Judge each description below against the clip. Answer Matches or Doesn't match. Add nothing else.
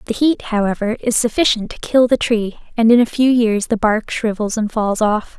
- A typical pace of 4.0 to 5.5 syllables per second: Matches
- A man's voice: Doesn't match